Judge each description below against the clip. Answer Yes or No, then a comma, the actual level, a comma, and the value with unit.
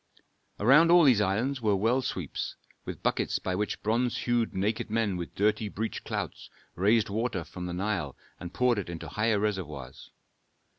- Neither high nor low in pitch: No, low, 105 Hz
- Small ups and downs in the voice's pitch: No, average, 3.7 semitones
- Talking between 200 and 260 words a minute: No, average, 165 wpm